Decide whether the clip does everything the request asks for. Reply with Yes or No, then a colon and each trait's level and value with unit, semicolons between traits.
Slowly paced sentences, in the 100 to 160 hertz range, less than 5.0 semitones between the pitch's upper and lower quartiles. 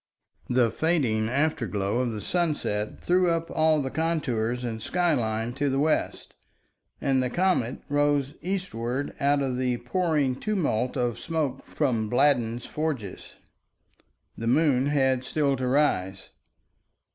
Yes: slow, 130 wpm; low, 135 Hz; average, 4.5 semitones